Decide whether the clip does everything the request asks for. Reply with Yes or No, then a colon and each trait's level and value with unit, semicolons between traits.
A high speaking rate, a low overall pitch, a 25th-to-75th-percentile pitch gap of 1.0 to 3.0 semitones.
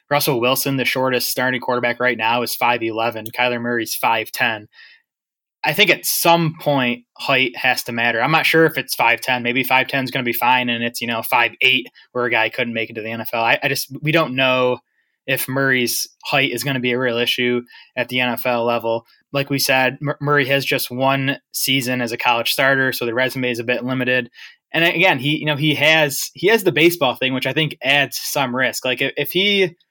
Yes: fast, 225 wpm; low, 130 Hz; narrow, 2.6 semitones